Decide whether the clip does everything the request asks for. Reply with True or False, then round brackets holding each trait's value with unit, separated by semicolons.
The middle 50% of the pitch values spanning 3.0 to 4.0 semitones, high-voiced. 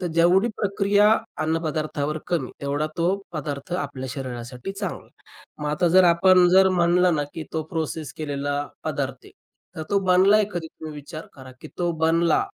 False (3.7 semitones; 165 Hz)